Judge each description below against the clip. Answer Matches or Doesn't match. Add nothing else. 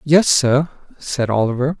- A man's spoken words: Matches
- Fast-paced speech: Doesn't match